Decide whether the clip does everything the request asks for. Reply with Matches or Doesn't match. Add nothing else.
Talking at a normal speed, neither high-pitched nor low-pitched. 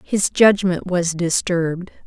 Doesn't match